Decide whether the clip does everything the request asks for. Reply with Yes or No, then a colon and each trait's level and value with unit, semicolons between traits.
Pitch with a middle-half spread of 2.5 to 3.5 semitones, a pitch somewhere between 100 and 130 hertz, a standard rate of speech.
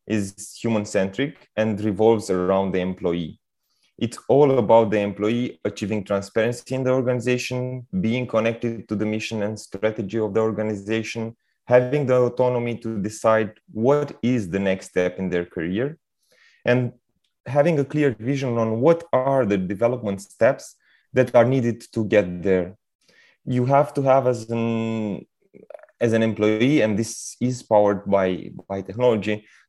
Yes: average, 3.2 semitones; low, 115 Hz; average, 150 wpm